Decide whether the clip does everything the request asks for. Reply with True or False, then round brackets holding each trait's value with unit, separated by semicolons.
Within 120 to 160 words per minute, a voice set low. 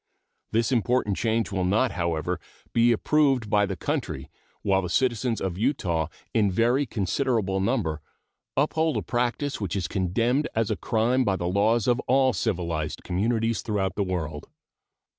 True (155 wpm; 110 Hz)